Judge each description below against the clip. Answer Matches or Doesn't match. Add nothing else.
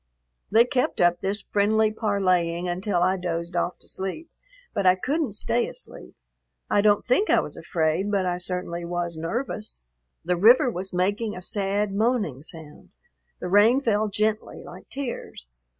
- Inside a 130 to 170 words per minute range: Matches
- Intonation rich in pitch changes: Doesn't match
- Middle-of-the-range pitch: Doesn't match